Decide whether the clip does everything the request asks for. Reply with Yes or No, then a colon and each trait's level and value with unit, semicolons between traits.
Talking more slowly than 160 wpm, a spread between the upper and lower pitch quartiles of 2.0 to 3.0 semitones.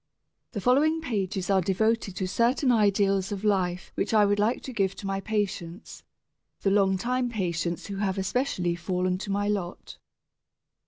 No: average, 165 wpm; narrow, 2.6 semitones